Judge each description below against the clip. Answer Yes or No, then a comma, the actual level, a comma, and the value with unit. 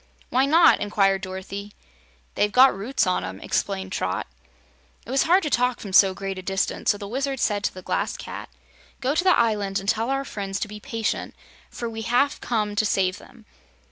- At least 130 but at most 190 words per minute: No, fast, 205 wpm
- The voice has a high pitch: Yes, high, 210 Hz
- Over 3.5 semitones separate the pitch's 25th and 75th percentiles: Yes, average, 4.4 semitones